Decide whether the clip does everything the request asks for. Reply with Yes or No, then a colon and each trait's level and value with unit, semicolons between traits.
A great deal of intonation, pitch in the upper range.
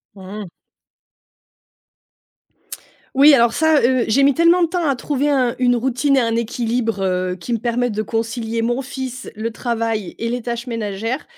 No: average, 2.8 semitones; high, 240 Hz